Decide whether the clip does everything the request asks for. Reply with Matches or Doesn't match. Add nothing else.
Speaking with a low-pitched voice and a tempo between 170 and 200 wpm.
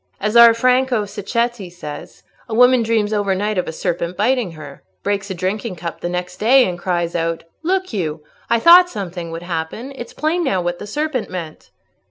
Doesn't match